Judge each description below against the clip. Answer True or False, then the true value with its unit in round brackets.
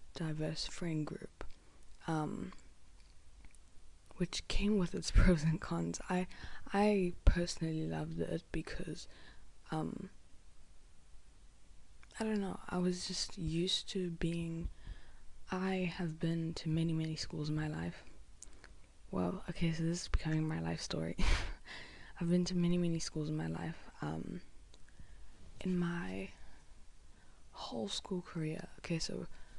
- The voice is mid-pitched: True (155 Hz)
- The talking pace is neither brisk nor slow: False (130 wpm)